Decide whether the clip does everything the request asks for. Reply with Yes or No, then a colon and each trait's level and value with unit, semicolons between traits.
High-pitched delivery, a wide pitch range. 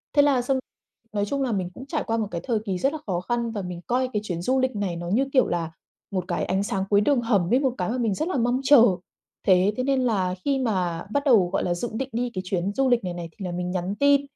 Yes: high, 215 Hz; wide, 6.1 semitones